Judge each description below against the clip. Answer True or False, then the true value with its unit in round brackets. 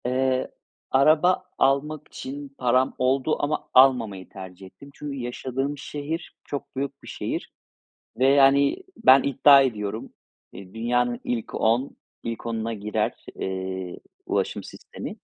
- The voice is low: True (130 Hz)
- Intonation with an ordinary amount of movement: True (3.6 semitones)